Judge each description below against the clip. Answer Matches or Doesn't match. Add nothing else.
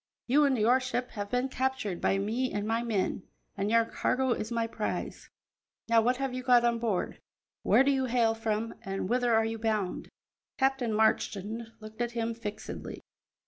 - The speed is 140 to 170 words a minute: Doesn't match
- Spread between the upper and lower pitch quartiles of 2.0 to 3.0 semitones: Matches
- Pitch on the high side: Matches